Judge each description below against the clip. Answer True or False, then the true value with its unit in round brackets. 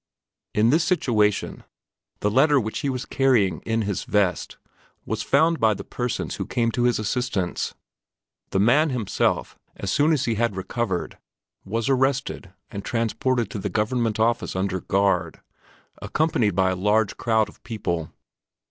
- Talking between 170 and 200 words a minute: False (155 wpm)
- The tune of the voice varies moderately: True (4.0 semitones)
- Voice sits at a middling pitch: False (110 Hz)